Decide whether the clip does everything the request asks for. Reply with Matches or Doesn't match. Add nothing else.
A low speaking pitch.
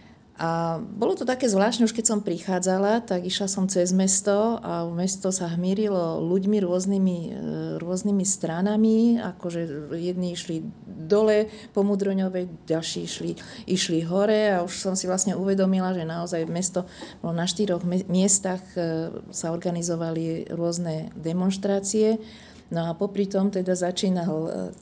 Doesn't match